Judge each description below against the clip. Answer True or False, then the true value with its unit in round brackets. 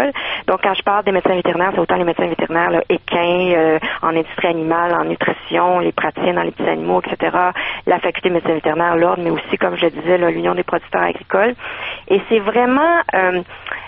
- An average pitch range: False (2.2 semitones)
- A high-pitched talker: False (180 Hz)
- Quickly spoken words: False (205 wpm)